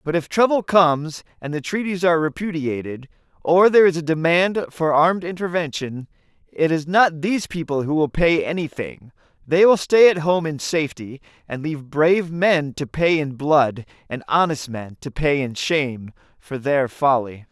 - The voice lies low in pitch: No, medium, 155 Hz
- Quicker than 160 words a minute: Yes, average, 175 wpm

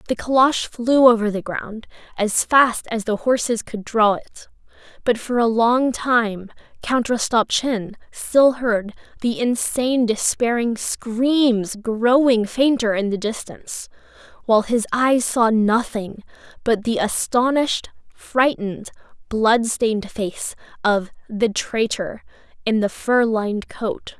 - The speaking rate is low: Yes, slow, 125 wpm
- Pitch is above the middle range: Yes, high, 230 Hz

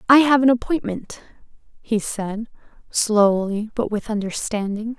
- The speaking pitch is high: Yes, high, 220 Hz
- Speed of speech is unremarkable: No, slow, 120 wpm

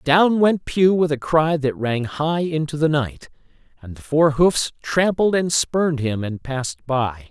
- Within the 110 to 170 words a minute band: No, average, 190 wpm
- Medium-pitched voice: Yes, medium, 150 Hz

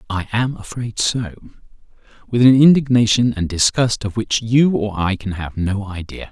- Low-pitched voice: Yes, low, 110 Hz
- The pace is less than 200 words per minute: Yes, average, 160 wpm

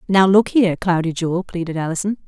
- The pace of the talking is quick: No, average, 185 wpm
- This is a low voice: No, medium, 180 Hz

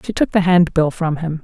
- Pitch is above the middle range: No, medium, 170 Hz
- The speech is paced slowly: No, fast, 250 wpm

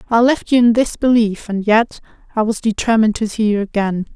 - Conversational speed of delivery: No, fast, 215 wpm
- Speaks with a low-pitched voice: No, high, 220 Hz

